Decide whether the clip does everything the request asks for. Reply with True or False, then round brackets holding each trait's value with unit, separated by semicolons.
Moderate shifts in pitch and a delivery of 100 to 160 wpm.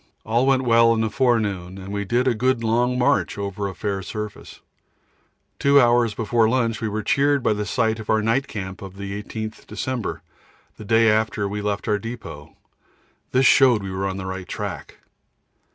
False (3.1 semitones; 190 wpm)